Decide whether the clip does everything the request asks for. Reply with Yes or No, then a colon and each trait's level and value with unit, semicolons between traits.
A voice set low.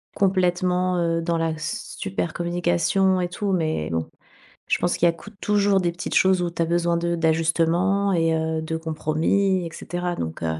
No: medium, 170 Hz